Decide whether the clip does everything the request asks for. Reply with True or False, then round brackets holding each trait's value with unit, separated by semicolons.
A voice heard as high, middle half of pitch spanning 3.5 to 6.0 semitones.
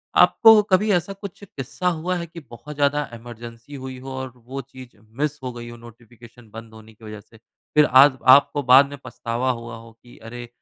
False (125 Hz; 3.9 semitones)